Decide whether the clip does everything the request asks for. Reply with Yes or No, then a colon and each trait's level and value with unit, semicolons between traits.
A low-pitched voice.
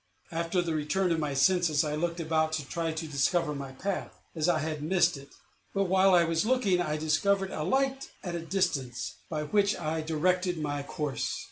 No: medium, 165 Hz